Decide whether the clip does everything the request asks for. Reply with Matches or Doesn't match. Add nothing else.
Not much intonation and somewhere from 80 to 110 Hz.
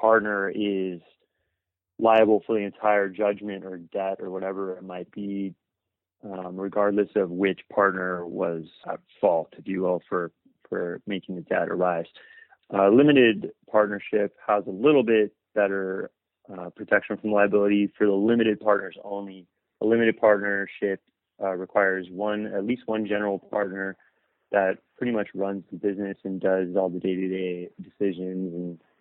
Matches